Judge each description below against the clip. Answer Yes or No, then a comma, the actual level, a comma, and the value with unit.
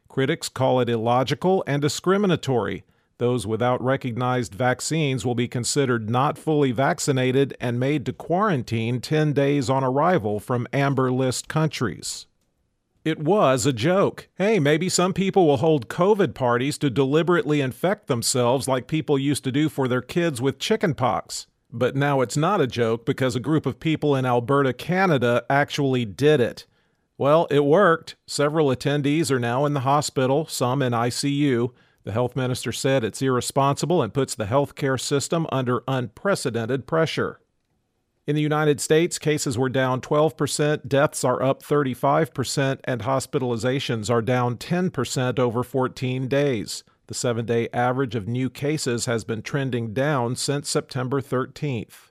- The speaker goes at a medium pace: Yes, average, 155 wpm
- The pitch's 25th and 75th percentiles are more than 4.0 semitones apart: No, average, 3.2 semitones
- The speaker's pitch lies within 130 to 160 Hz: Yes, low, 135 Hz